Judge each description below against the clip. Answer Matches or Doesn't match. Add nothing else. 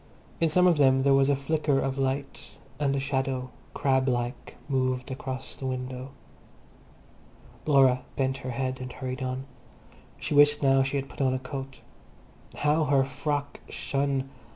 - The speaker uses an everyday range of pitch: Doesn't match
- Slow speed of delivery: Doesn't match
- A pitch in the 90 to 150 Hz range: Matches